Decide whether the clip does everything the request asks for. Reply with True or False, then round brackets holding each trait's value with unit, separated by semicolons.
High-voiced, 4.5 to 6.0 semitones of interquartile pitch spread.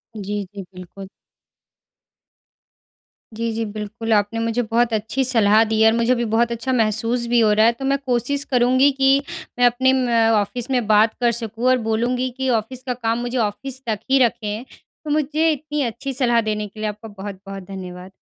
False (230 Hz; 2.8 semitones)